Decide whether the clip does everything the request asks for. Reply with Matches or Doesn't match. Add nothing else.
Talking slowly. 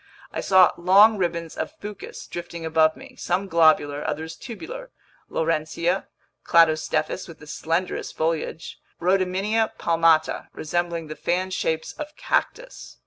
Matches